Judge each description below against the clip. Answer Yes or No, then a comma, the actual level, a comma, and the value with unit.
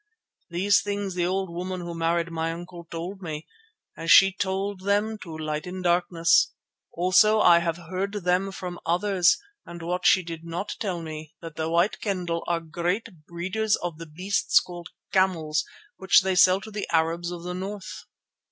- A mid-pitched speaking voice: Yes, medium, 175 Hz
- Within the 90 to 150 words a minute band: No, average, 175 wpm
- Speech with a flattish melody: Yes, narrow, 2.2 semitones